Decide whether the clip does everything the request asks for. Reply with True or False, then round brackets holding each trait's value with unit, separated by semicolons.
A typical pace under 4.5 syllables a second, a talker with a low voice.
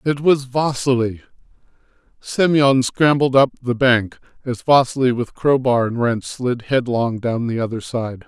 True (4.3 syllables/s; 125 Hz)